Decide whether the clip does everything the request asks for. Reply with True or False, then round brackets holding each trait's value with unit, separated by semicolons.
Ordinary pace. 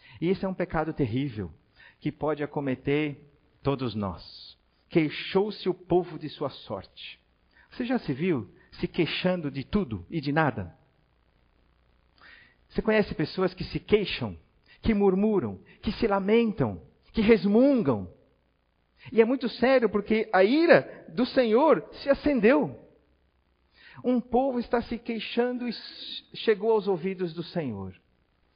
True (130 wpm)